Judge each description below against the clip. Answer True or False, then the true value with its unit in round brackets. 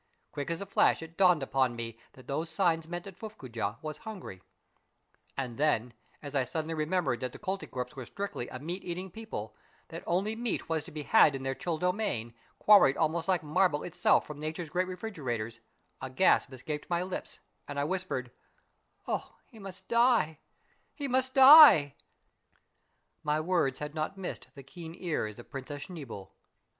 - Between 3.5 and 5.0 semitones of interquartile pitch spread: False (5.6 semitones)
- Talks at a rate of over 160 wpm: True (185 wpm)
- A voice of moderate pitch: True (160 Hz)